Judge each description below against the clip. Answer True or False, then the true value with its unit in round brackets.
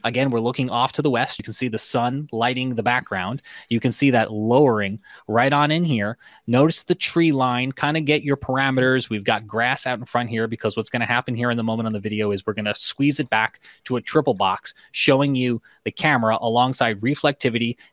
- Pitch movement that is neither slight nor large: True (3.4 semitones)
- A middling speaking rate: False (230 wpm)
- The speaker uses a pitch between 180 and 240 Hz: False (120 Hz)